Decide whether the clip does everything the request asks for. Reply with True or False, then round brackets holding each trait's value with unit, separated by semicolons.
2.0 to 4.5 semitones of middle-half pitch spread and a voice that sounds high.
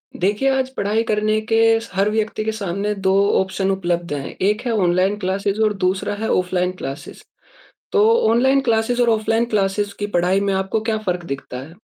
True (2.9 semitones; 205 Hz)